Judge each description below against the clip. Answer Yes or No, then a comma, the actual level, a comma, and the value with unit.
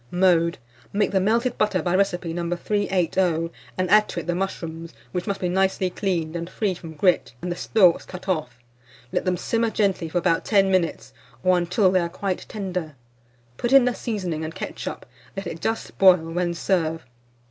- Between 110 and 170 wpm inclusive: No, average, 190 wpm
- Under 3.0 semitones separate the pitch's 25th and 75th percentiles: Yes, narrow, 2.5 semitones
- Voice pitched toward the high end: No, medium, 180 Hz